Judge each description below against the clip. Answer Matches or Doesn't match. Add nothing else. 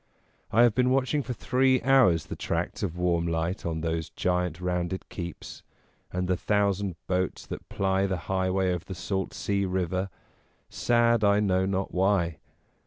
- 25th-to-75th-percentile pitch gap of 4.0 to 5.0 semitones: Doesn't match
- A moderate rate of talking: Matches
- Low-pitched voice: Matches